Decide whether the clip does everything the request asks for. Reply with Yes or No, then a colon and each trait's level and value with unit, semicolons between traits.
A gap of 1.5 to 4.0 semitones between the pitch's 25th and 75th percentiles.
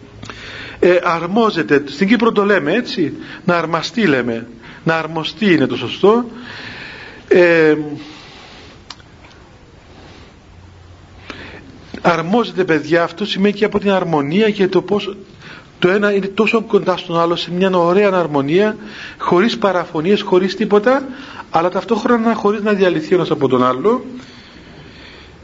No: average, 5.2 semitones